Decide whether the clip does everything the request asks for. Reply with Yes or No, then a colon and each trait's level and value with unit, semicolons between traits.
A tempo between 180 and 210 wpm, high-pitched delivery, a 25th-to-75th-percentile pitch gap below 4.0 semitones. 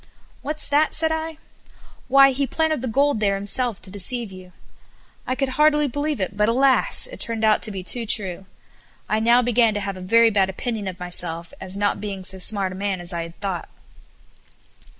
No: average, 200 wpm; high, 215 Hz; wide, 5.5 semitones